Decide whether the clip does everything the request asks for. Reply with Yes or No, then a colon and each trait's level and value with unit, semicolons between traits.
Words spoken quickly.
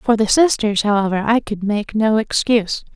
No: average, 180 wpm